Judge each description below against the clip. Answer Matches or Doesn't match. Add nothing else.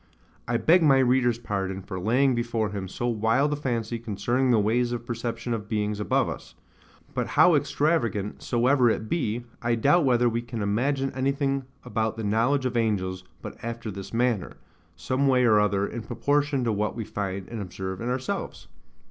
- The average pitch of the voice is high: Doesn't match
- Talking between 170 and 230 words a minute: Matches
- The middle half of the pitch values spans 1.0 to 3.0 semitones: Doesn't match